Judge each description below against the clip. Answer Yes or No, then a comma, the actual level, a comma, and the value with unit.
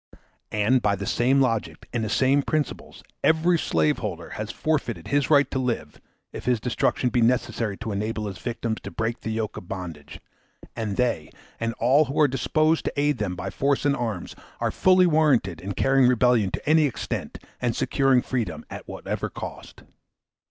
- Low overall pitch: Yes, low, 120 Hz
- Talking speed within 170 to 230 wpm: Yes, average, 180 wpm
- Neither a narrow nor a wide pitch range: Yes, average, 4.6 semitones